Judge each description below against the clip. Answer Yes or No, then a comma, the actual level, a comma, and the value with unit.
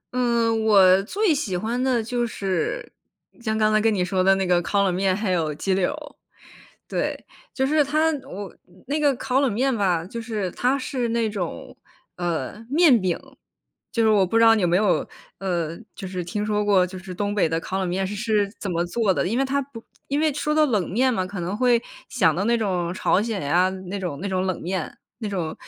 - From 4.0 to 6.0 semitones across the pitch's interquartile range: Yes, average, 4.5 semitones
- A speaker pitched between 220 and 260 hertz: No, high, 205 Hz